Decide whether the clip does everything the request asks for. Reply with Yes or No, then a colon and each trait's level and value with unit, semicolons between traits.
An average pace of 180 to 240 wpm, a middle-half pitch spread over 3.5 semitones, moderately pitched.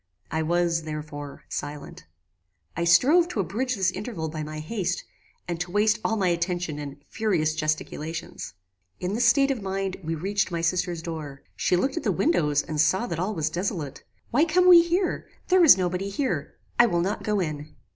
Yes: average, 190 wpm; wide, 5.4 semitones; medium, 180 Hz